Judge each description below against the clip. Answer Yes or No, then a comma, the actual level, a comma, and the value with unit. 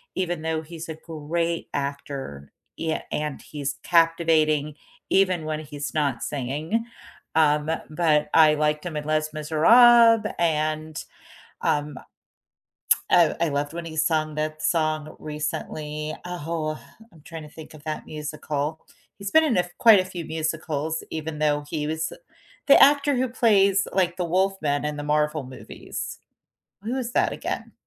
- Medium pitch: Yes, medium, 155 Hz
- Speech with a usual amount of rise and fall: No, narrow, 2.3 semitones